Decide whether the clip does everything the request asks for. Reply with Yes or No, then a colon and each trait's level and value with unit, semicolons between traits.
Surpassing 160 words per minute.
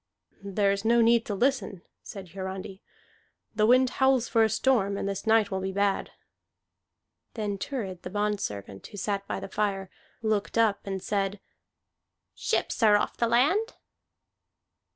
No: average, 150 wpm